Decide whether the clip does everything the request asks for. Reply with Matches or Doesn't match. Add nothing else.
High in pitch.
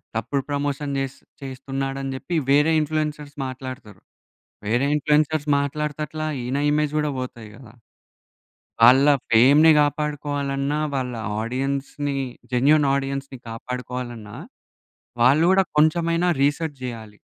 Doesn't match